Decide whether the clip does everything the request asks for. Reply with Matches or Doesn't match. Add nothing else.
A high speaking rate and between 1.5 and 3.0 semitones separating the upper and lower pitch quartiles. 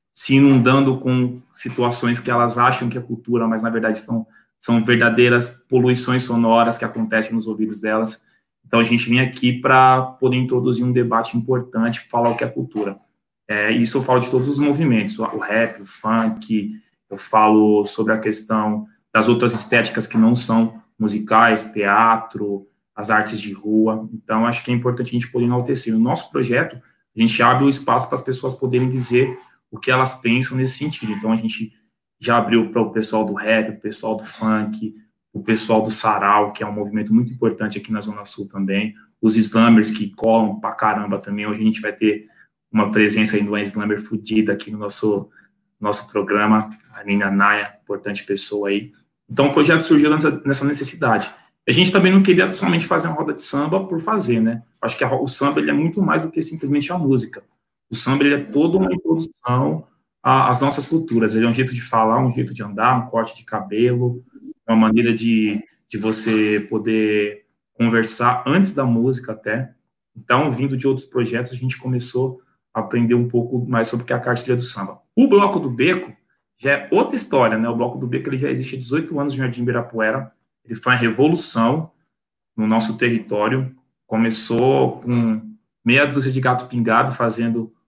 Matches